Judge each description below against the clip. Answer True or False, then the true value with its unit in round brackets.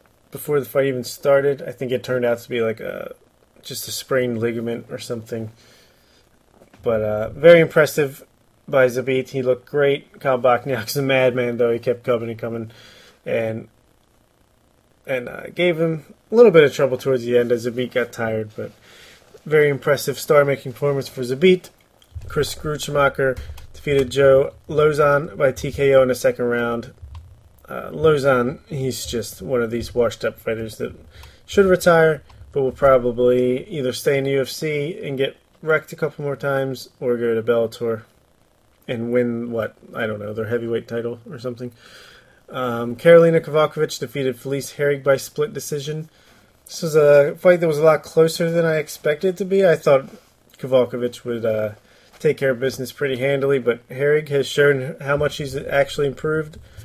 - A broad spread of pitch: False (3.4 semitones)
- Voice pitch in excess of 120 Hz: True (130 Hz)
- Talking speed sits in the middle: True (170 wpm)